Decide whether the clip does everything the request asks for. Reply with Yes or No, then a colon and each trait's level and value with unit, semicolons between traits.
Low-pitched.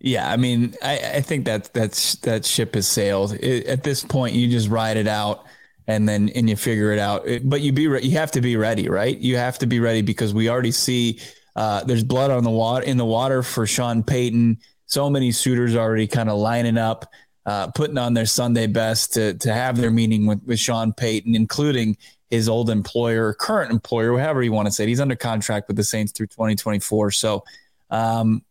Yes: low, 115 Hz